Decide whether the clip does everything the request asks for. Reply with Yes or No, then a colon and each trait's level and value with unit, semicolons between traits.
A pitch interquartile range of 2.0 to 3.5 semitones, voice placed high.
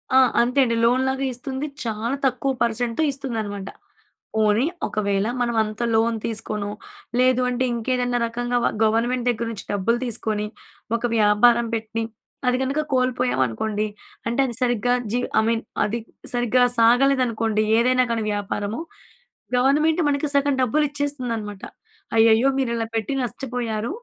Yes: narrow, 2.6 semitones; high, 235 Hz